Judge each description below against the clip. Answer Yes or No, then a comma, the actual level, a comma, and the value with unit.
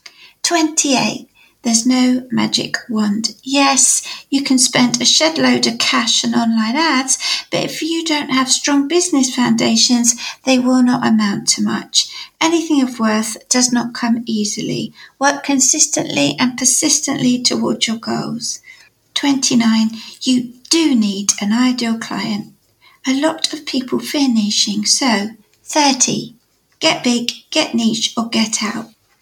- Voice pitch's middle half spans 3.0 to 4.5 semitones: Yes, average, 3.9 semitones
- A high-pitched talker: Yes, very high, 250 Hz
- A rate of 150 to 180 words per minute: No, average, 140 wpm